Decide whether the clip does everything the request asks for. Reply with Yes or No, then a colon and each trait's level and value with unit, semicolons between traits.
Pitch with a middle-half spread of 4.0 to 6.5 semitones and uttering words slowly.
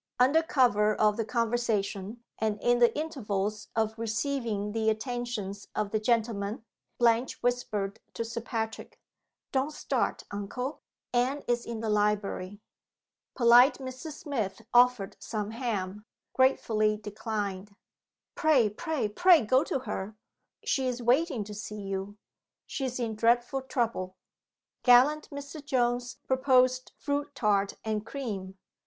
No: average, 3.5 semitones; slow, 130 wpm